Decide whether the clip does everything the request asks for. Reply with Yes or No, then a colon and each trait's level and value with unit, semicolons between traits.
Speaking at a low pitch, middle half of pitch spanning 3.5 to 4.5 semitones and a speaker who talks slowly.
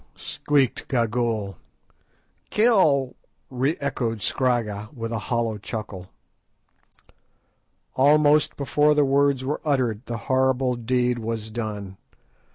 Yes: low, 125 Hz; average, 3.8 semitones; slow, 105 wpm